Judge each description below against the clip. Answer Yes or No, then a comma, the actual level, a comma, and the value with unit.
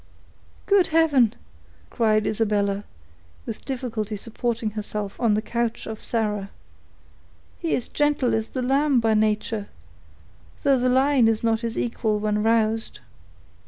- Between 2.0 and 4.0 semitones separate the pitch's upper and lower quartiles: Yes, average, 2.8 semitones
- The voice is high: Yes, high, 225 Hz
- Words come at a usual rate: No, slow, 130 wpm